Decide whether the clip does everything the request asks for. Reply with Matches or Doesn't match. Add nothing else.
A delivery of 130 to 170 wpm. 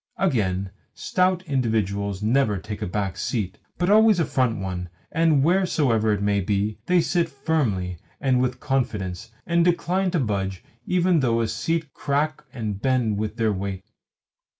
Matches